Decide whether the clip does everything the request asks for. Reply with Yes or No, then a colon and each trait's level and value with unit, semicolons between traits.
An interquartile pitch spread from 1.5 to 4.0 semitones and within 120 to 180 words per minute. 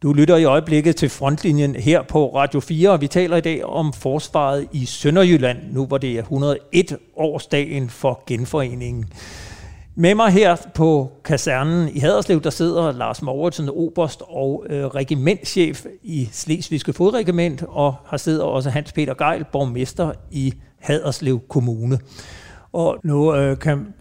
Yes: average, 3.5 semitones; average, 150 wpm